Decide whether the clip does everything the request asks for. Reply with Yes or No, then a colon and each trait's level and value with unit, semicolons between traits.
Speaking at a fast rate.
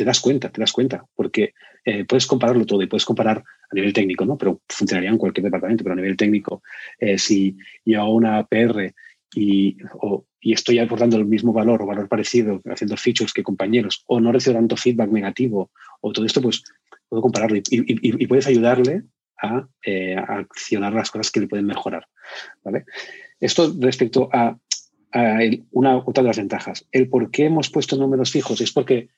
Yes: fast, 195 wpm